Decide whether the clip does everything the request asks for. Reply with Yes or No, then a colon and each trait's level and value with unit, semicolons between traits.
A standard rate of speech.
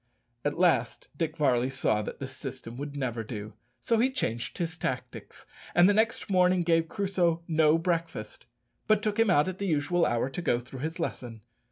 Yes: average, 190 wpm